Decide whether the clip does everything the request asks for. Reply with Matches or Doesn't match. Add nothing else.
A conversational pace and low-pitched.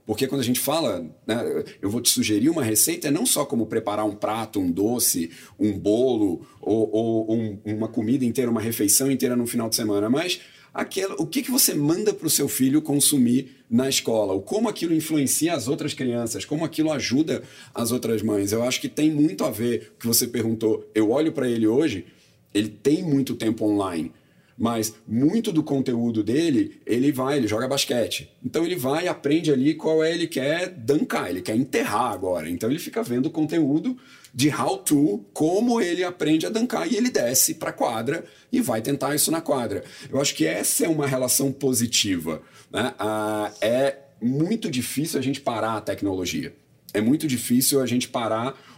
Doesn't match